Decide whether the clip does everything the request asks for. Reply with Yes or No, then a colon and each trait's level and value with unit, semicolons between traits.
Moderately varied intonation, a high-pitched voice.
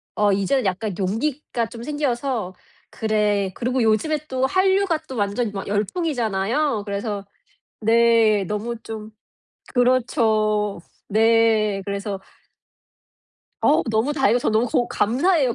Yes: average, 3.7 semitones; high, 225 Hz